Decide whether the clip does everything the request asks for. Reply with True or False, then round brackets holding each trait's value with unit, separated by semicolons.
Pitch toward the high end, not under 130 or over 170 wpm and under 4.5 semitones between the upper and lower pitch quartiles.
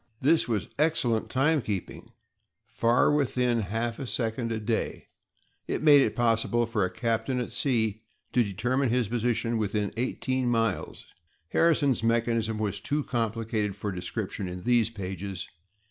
False (115 Hz; 135 wpm; 2.6 semitones)